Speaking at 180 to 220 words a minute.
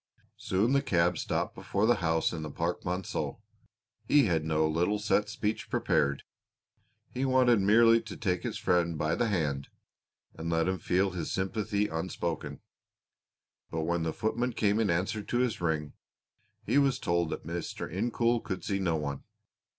No: average, 165 wpm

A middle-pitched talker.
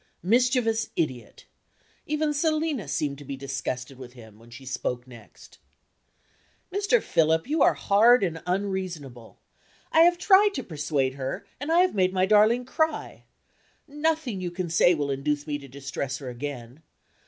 Yes: medium, 170 Hz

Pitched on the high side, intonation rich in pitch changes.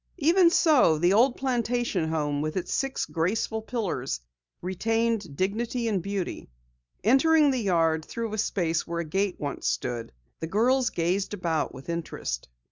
Yes: high, 200 Hz; wide, 6.3 semitones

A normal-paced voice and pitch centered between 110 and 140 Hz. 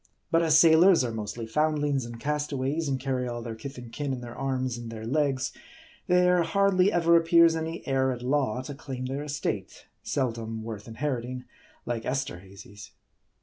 Yes: average, 170 wpm; low, 135 Hz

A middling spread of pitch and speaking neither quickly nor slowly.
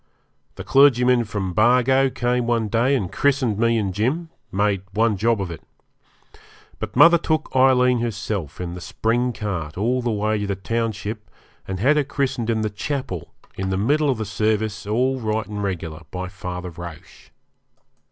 Yes: average, 4.3 semitones; average, 170 wpm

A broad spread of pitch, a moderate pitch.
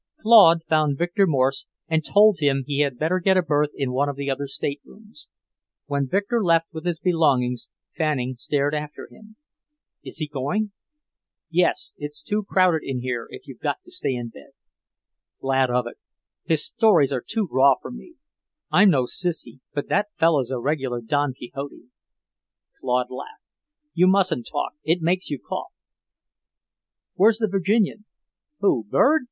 Yes: wide, 5.8 semitones; medium, 150 Hz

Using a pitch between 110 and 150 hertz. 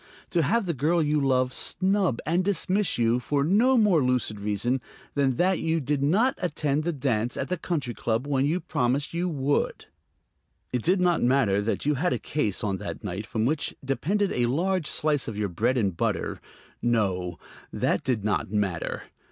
Yes: medium, 140 Hz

